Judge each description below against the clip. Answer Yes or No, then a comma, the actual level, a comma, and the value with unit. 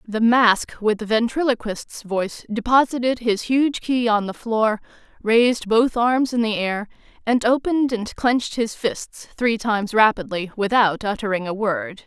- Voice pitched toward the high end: Yes, high, 225 Hz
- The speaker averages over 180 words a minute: No, average, 160 wpm